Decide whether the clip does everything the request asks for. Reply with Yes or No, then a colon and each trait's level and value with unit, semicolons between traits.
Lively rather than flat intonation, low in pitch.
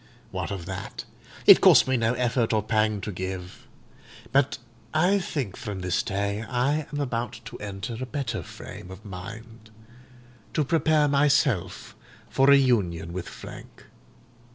Yes: wide, 5.8 semitones; low, 115 Hz